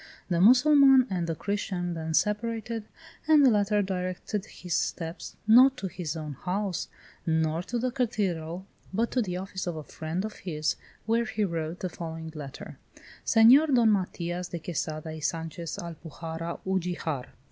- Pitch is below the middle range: No, medium, 180 Hz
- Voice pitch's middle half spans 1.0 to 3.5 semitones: No, average, 5.0 semitones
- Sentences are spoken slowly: No, average, 160 wpm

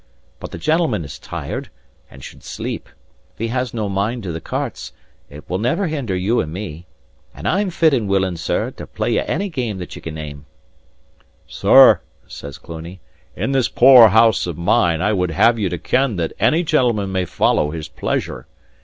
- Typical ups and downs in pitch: No, wide, 6.8 semitones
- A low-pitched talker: Yes, low, 100 Hz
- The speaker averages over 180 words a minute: Yes, average, 190 wpm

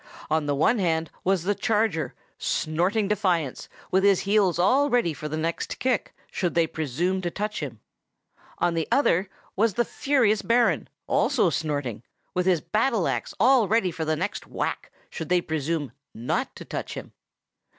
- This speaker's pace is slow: No, average, 175 wpm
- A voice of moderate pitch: Yes, medium, 180 Hz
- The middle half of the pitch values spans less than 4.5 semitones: No, average, 5.0 semitones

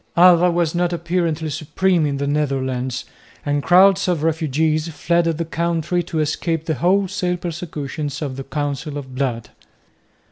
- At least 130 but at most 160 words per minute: Yes, average, 145 wpm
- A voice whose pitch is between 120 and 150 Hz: No, medium, 160 Hz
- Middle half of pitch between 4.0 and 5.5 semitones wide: No, average, 3.1 semitones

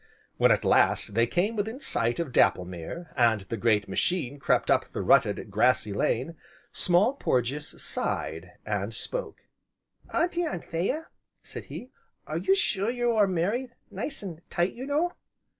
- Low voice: No, medium, 175 Hz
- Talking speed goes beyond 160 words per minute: No, average, 155 wpm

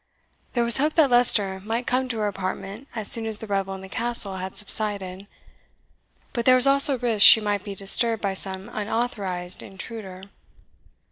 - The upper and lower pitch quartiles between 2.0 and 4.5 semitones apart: Yes, average, 3.6 semitones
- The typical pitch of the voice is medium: No, high, 210 Hz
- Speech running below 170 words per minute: No, average, 180 wpm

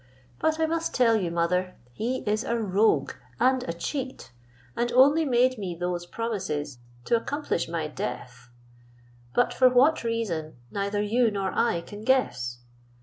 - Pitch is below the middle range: No, high, 215 Hz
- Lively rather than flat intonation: Yes, wide, 6.7 semitones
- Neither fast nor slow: Yes, average, 150 wpm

